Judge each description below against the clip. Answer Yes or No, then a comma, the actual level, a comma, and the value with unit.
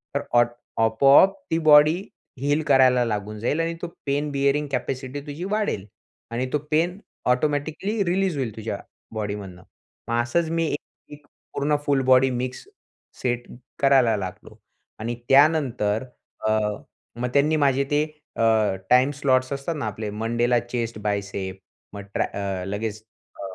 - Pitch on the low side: Yes, low, 130 Hz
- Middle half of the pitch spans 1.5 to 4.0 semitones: No, average, 4.7 semitones